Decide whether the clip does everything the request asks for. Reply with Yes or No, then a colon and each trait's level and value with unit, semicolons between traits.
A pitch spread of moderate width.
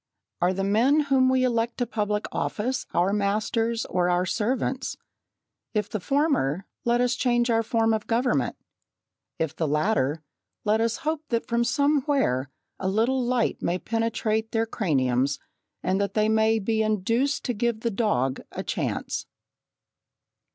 Yes: average, 3.8 semitones